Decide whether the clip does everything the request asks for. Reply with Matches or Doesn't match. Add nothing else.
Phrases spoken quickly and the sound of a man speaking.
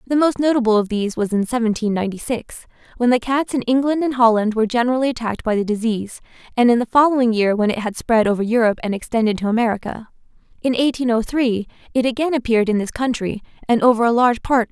Doesn't match